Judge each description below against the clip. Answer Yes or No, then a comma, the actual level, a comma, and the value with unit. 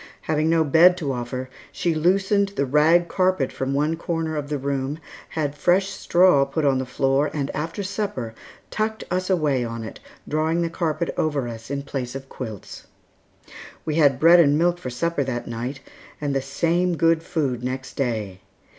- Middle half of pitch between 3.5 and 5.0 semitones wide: Yes, average, 4.2 semitones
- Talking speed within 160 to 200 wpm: Yes, average, 180 wpm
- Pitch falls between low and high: Yes, medium, 150 Hz